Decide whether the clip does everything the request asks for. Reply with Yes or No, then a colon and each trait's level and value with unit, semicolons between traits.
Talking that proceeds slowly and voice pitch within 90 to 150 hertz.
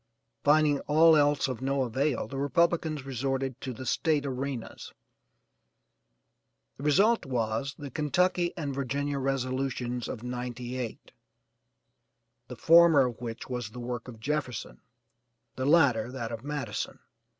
Yes: slow, 130 wpm; low, 135 Hz